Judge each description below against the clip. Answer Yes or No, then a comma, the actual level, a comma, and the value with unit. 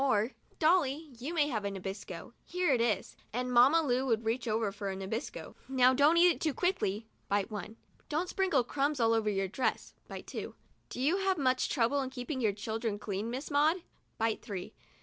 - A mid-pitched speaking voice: No, high, 245 Hz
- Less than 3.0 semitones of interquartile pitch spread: No, wide, 5.4 semitones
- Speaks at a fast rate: Yes, fast, 215 wpm